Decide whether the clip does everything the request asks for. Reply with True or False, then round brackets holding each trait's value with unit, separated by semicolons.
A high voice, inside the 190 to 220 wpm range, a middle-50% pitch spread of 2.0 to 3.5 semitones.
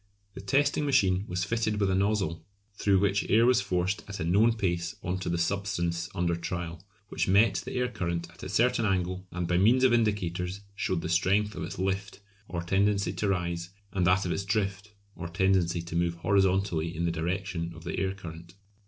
False (95 Hz; 205 wpm; 2.7 semitones)